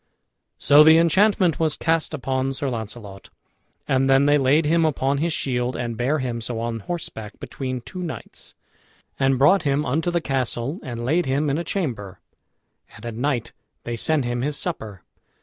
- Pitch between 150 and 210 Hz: No, low, 135 Hz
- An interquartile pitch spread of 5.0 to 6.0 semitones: No, average, 4.6 semitones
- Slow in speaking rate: No, average, 175 wpm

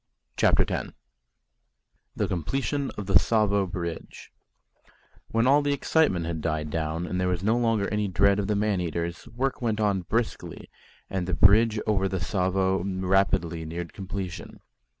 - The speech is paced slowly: No, average, 155 wpm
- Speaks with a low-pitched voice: Yes, very low, 95 Hz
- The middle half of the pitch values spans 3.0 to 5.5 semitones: Yes, average, 3.7 semitones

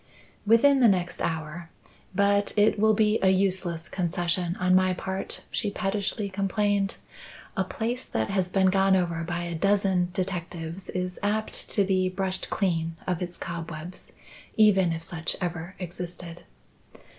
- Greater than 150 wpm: No, average, 145 wpm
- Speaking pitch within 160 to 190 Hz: Yes, medium, 185 Hz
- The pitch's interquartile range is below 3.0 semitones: Yes, narrow, 2.4 semitones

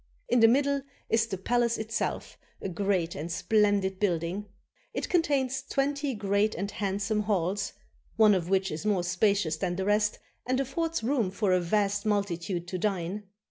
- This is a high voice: Yes, high, 205 Hz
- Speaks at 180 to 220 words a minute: No, average, 165 wpm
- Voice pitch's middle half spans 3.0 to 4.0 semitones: Yes, average, 3.3 semitones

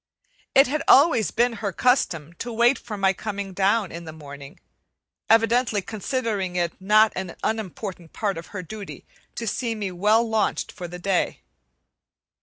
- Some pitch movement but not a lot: Yes, average, 4.1 semitones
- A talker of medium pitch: No, high, 210 Hz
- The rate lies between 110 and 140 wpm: No, average, 160 wpm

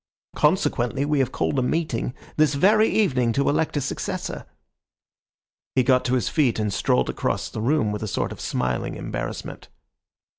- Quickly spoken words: No, average, 170 wpm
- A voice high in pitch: No, low, 130 Hz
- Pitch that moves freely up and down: No, average, 4.6 semitones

